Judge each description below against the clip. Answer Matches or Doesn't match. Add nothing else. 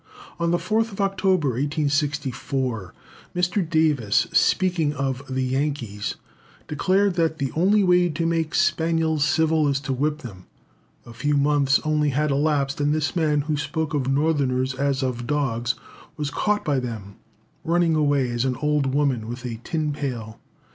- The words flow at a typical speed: Matches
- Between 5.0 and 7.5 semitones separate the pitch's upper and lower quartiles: Doesn't match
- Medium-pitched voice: Matches